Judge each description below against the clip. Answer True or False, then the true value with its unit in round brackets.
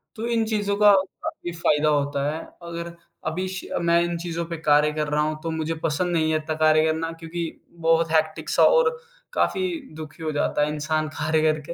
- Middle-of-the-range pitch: True (160 Hz)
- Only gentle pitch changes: True (1.7 semitones)